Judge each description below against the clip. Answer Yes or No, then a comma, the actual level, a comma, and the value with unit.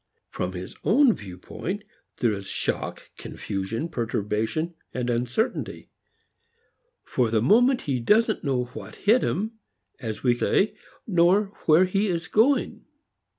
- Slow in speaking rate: Yes, slow, 120 wpm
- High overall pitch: No, medium, 160 Hz